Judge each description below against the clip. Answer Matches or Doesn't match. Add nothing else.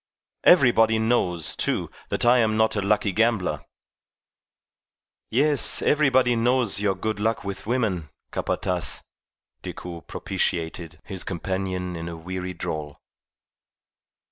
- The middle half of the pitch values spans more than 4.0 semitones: Matches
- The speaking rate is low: Matches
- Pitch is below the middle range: Matches